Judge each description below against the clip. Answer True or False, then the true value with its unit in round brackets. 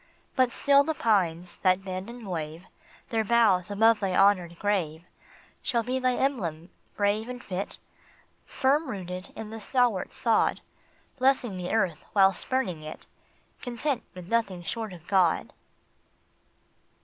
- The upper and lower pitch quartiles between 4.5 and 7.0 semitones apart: True (4.8 semitones)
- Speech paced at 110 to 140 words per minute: True (135 wpm)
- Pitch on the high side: True (205 Hz)